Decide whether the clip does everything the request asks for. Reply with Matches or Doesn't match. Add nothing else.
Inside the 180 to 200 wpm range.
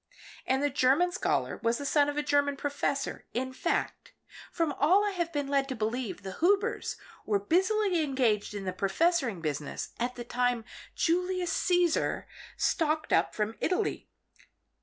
Doesn't match